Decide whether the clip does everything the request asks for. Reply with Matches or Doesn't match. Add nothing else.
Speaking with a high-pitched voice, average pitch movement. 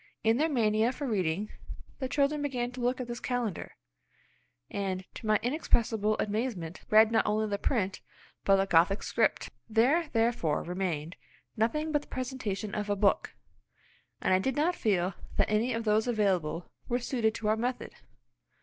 Matches